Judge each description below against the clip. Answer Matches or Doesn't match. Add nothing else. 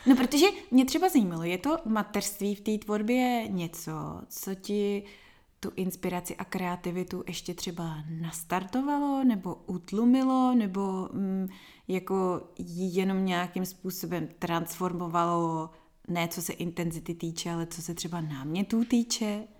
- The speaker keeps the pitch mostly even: Doesn't match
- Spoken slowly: Doesn't match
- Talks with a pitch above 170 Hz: Matches